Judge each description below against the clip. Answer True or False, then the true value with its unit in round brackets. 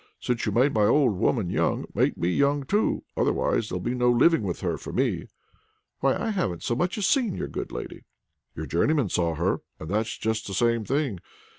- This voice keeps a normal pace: False (210 wpm)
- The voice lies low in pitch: True (120 Hz)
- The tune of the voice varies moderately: False (6.6 semitones)